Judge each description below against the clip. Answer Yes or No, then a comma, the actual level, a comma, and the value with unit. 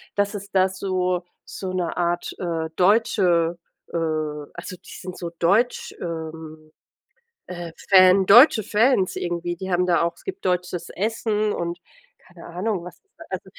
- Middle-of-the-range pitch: Yes, medium, 180 Hz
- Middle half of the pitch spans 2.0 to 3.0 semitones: Yes, narrow, 2.4 semitones